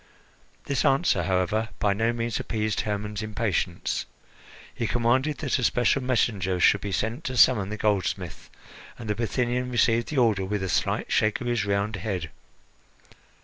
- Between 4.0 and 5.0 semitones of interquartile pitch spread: No, average, 3.2 semitones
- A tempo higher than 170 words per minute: No, average, 160 wpm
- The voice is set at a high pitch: No, low, 110 Hz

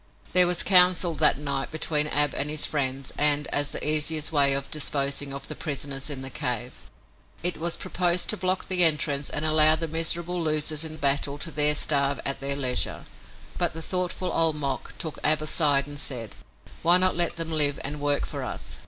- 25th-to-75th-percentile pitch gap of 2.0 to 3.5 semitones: Yes, average, 2.7 semitones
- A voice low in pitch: No, medium, 150 Hz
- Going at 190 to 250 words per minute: Yes, average, 195 wpm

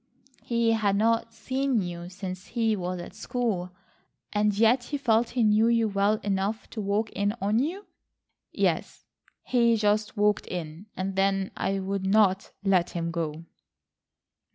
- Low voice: No, high, 205 Hz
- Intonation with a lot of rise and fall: No, average, 3.0 semitones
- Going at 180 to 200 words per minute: No, average, 155 wpm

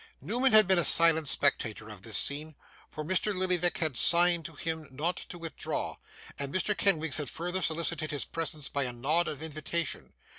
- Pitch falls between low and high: Yes, medium, 160 Hz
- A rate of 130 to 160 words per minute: No, average, 185 wpm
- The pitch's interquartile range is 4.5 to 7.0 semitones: No, average, 3.3 semitones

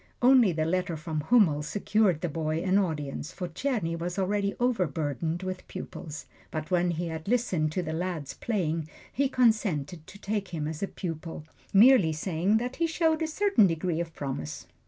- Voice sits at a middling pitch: Yes, medium, 175 Hz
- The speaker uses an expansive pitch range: No, average, 4.8 semitones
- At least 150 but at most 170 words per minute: No, average, 180 wpm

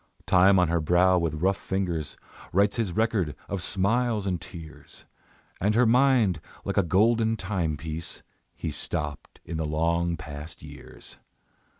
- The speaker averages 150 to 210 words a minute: No, average, 140 wpm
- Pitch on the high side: No, very low, 90 Hz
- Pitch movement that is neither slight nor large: Yes, average, 4.0 semitones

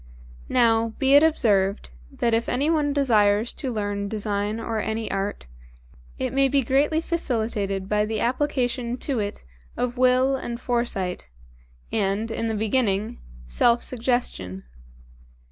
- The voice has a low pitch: No, high, 230 Hz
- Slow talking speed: Yes, slow, 130 wpm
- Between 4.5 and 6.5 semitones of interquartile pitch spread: No, average, 3.7 semitones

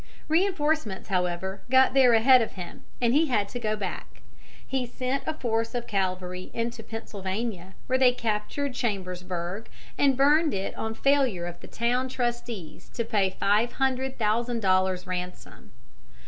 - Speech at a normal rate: Yes, average, 150 wpm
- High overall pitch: Yes, high, 230 Hz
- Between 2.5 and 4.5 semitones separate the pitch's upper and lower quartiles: No, average, 5.3 semitones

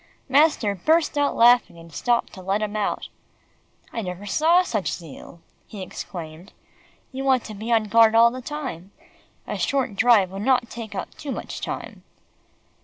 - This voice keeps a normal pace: Yes, average, 170 wpm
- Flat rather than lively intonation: No, average, 5.0 semitones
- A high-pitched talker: Yes, high, 225 Hz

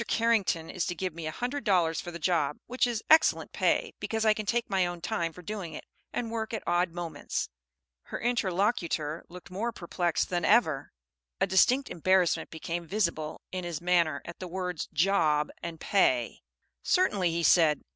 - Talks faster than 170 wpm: Yes, average, 180 wpm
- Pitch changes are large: No, average, 4.2 semitones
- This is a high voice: No, medium, 180 Hz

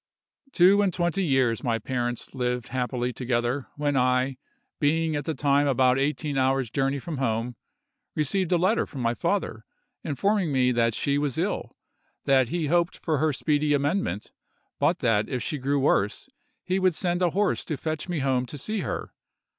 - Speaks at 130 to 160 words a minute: No, average, 170 wpm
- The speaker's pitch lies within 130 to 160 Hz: Yes, medium, 140 Hz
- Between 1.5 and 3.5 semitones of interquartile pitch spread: No, average, 4.3 semitones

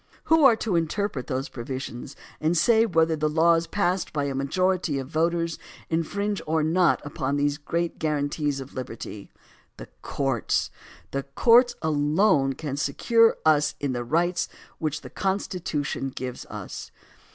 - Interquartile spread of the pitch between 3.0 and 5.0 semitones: Yes, average, 4.4 semitones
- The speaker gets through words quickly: No, average, 145 wpm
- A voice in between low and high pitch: Yes, medium, 155 Hz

